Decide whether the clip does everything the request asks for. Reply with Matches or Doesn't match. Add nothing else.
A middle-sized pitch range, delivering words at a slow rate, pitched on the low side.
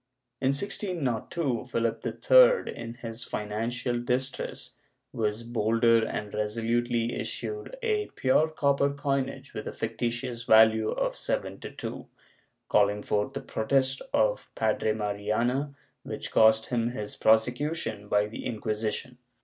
Matches